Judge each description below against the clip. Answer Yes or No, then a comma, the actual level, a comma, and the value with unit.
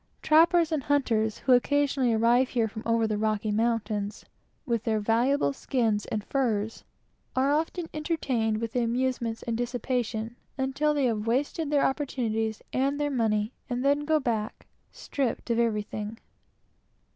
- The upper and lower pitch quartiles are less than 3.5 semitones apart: No, average, 4.0 semitones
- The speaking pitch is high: Yes, high, 240 Hz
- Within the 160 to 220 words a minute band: No, average, 150 wpm